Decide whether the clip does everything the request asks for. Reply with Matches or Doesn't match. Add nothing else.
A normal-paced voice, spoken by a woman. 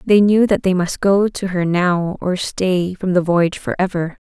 Doesn't match